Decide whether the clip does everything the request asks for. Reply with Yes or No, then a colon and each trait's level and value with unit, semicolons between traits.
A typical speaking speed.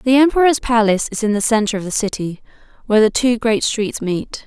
No: fast, 215 wpm